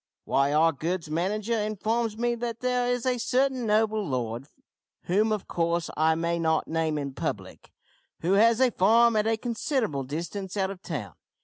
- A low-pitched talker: No, high, 200 Hz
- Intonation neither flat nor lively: No, wide, 6.2 semitones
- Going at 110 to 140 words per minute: No, average, 175 wpm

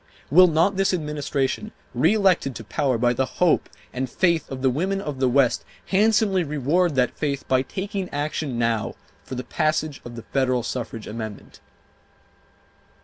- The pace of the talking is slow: No, average, 155 wpm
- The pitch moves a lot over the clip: Yes, wide, 5.9 semitones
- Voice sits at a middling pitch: Yes, medium, 145 Hz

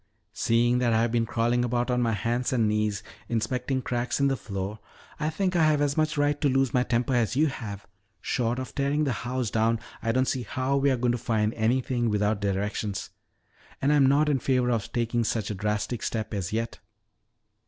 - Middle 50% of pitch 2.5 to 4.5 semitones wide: Yes, average, 3.1 semitones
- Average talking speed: No, fast, 215 wpm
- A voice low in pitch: Yes, low, 120 Hz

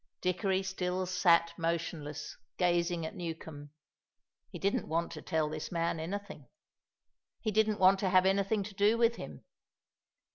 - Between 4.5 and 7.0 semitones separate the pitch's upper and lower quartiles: No, average, 2.9 semitones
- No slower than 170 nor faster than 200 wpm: No, average, 145 wpm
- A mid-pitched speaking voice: Yes, medium, 180 Hz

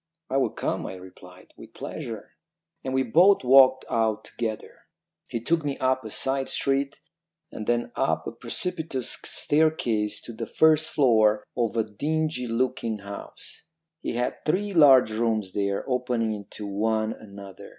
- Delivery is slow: No, average, 150 wpm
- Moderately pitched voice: No, low, 120 Hz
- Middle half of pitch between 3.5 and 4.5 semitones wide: Yes, average, 4.1 semitones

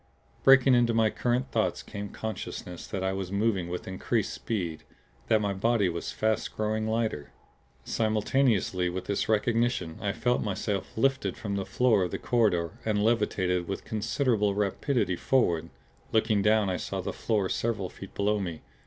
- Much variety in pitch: No, average, 3.3 semitones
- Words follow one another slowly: No, average, 165 wpm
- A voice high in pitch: No, low, 105 Hz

